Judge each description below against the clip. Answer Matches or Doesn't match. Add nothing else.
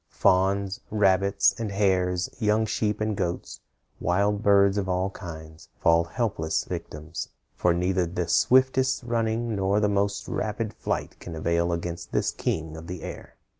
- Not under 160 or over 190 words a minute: Doesn't match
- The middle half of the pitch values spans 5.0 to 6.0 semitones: Doesn't match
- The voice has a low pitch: Matches